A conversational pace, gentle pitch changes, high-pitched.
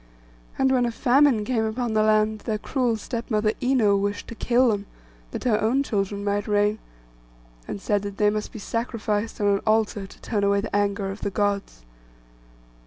Yes: average, 190 wpm; narrow, 2.3 semitones; high, 215 Hz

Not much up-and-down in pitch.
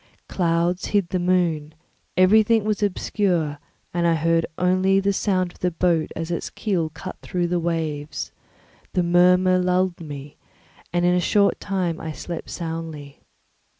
Yes: narrow, 2.1 semitones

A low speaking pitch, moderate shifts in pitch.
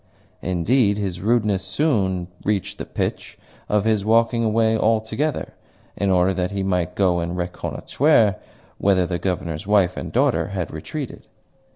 Yes: low, 100 Hz; average, 3.6 semitones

